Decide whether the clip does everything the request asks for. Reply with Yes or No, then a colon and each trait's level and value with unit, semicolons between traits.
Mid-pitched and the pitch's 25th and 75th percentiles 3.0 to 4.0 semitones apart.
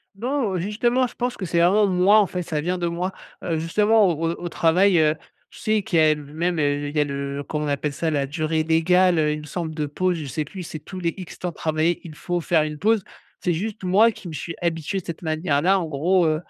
Yes: medium, 170 Hz; average, 3.3 semitones